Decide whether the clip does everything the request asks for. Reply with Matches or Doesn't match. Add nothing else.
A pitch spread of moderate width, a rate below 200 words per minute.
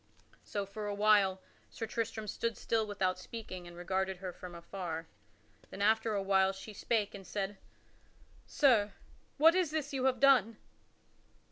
Matches